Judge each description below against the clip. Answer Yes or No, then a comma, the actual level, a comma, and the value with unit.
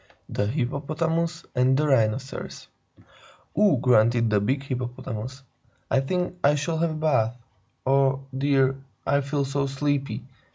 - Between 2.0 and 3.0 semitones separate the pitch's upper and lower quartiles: Yes, average, 2.7 semitones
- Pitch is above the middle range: No, low, 135 Hz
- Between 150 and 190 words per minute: No, average, 140 wpm